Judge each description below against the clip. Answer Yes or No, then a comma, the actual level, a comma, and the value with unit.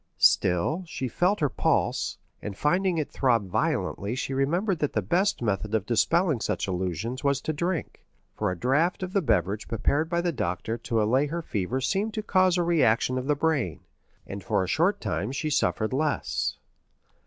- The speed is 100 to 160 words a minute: No, average, 185 wpm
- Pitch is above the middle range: No, low, 135 Hz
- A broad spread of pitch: Yes, wide, 7.9 semitones